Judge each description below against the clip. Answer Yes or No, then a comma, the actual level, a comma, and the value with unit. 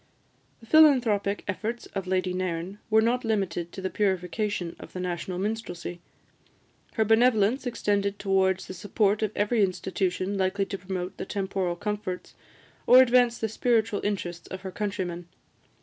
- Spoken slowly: No, average, 150 wpm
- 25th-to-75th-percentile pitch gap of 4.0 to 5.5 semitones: No, average, 3.0 semitones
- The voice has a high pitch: Yes, high, 200 Hz